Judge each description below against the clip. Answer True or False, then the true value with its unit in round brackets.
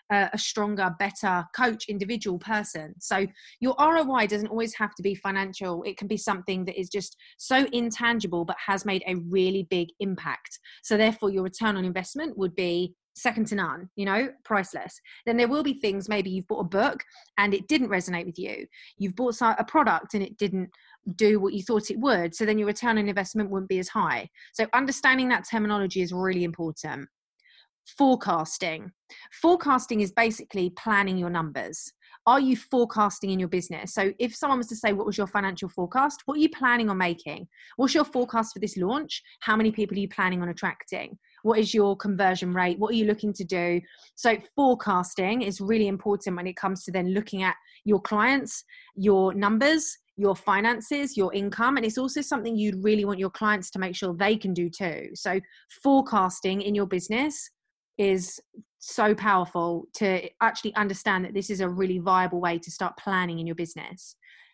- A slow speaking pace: False (190 wpm)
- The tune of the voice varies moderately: True (3.4 semitones)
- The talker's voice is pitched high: True (205 Hz)